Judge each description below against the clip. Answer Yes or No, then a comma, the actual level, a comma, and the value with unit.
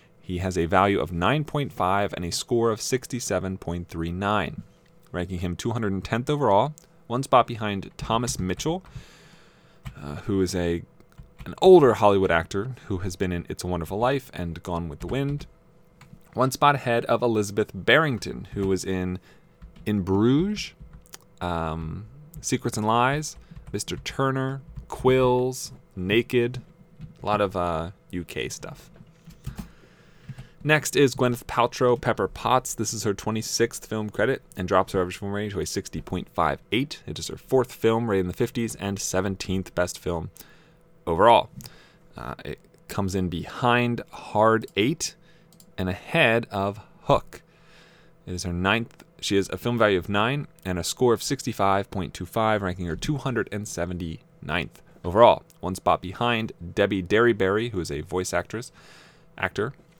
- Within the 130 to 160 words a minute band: Yes, average, 145 wpm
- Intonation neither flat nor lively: No, wide, 6.1 semitones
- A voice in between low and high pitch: No, low, 110 Hz